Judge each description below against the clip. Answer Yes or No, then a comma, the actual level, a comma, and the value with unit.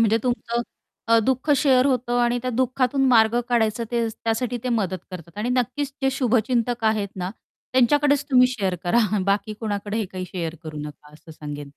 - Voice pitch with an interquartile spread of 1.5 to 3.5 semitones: No, average, 4.1 semitones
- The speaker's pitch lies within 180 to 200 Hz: No, high, 230 Hz